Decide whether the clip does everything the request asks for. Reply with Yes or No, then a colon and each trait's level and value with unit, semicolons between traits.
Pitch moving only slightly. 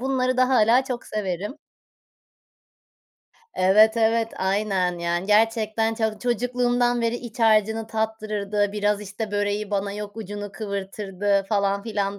Yes: narrow, 2.1 semitones